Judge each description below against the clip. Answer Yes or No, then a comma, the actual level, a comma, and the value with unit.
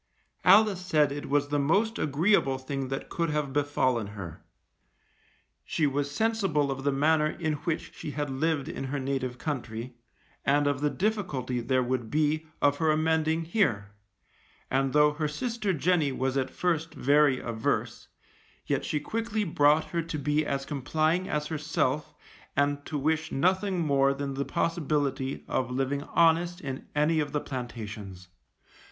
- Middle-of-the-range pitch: Yes, medium, 145 Hz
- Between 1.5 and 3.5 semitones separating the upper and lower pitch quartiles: Yes, average, 3.1 semitones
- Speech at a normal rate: Yes, average, 160 wpm